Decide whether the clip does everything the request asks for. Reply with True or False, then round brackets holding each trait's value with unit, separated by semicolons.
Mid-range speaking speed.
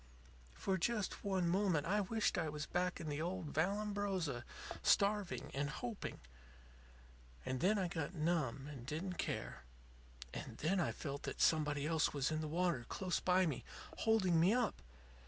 True (160 wpm)